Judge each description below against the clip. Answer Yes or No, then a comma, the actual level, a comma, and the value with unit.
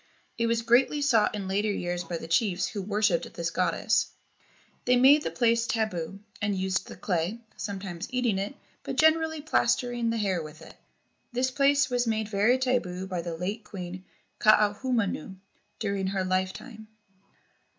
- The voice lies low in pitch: No, high, 210 Hz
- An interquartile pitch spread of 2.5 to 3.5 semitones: No, average, 4.6 semitones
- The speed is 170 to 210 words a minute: No, average, 160 wpm